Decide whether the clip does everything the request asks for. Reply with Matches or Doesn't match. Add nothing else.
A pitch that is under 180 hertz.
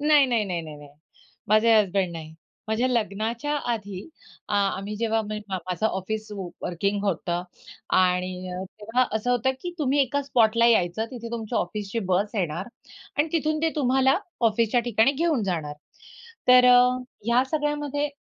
Doesn't match